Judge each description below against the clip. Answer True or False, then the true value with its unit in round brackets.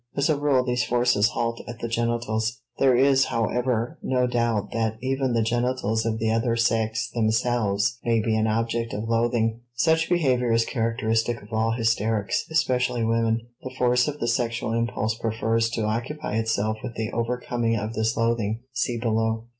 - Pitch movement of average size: False (1.6 semitones)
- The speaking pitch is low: True (115 Hz)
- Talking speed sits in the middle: True (170 wpm)